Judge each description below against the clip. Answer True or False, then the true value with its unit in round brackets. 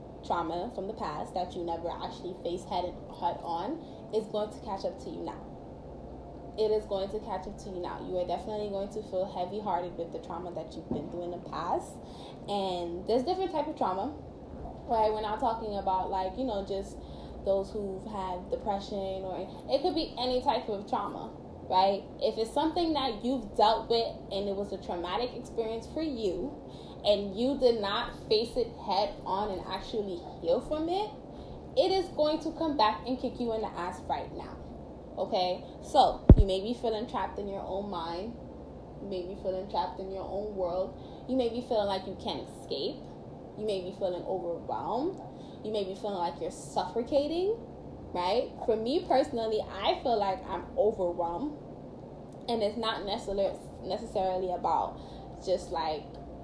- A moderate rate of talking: True (185 wpm)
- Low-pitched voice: False (205 Hz)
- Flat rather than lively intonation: False (4.5 semitones)